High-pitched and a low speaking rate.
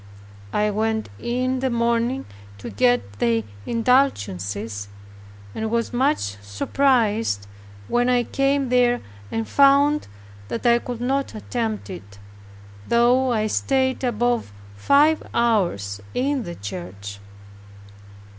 Yes: high, 235 Hz; slow, 110 wpm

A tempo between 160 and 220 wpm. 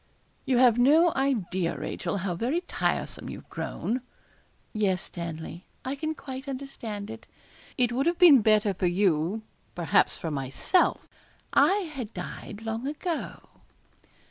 No: slow, 135 wpm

